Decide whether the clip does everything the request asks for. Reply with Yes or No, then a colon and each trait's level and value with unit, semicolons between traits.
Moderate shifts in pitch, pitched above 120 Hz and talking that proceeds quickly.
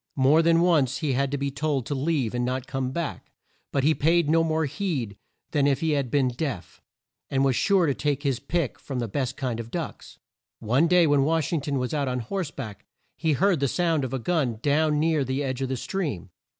Yes: average, 3.5 semitones; medium, 140 Hz; fast, 230 wpm